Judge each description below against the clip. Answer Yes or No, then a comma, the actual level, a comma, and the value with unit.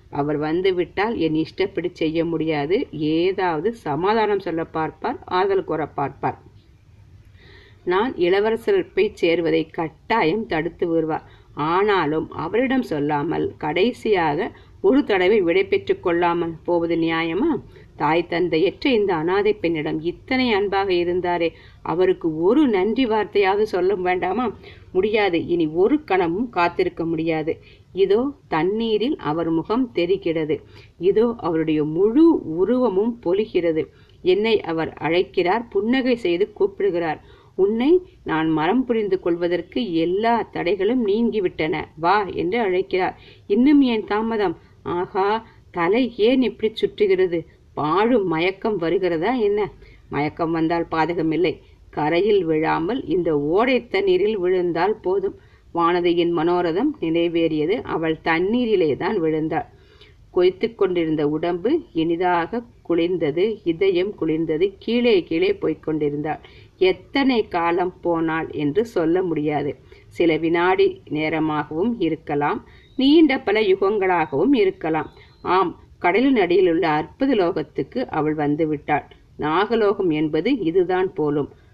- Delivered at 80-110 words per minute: Yes, average, 105 wpm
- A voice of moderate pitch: No, high, 200 Hz